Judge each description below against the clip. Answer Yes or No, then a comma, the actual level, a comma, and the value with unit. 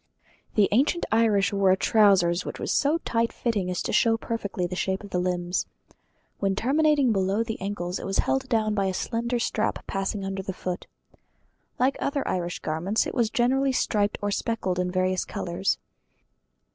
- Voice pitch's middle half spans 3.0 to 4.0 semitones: Yes, average, 3.7 semitones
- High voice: Yes, high, 200 Hz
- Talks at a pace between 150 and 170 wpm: No, average, 180 wpm